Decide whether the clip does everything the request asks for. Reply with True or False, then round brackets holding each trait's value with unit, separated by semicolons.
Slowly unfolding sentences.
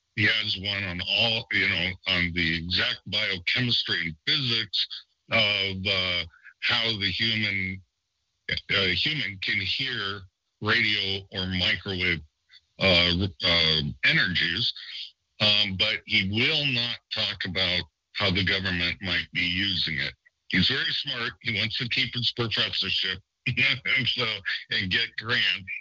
True (130 wpm)